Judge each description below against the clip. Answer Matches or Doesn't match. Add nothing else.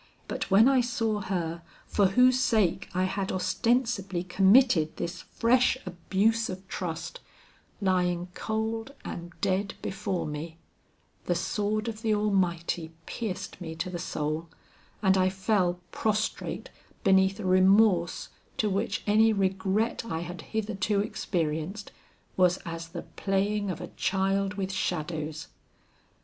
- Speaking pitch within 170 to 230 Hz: Matches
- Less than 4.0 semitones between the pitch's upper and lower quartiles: Matches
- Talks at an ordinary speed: Doesn't match